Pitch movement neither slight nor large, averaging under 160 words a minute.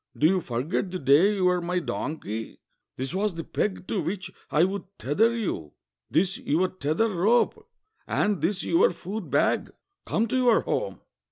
No: average, 4.5 semitones; average, 170 wpm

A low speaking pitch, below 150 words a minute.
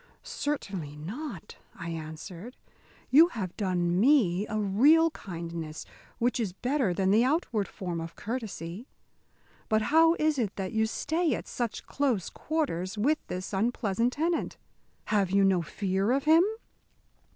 No: high, 210 Hz; average, 140 wpm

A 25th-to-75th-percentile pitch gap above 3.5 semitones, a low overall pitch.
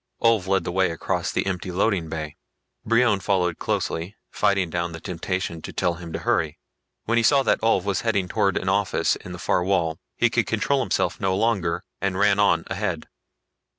No: average, 3.2 semitones; very low, 95 Hz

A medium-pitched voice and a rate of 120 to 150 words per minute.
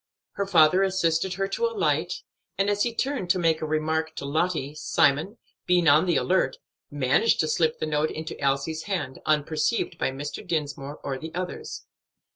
No: medium, 160 Hz; average, 175 wpm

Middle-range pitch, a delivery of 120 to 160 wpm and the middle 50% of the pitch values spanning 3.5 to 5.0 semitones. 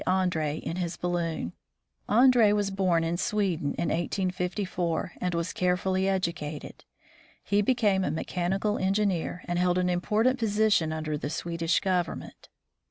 No: medium, 180 Hz; slow, 135 wpm; average, 2.7 semitones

